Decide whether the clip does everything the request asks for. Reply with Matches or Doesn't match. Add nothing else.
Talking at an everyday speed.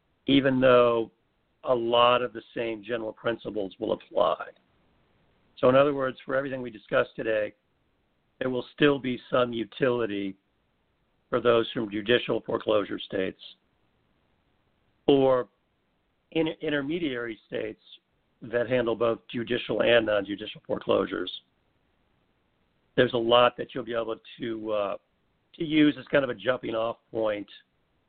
Doesn't match